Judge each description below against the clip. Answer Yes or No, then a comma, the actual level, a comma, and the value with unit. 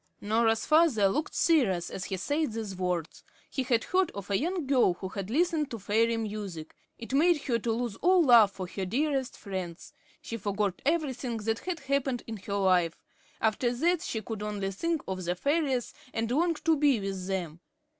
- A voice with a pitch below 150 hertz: No, high, 225 Hz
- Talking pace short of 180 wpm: No, average, 185 wpm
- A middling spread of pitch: No, wide, 6.6 semitones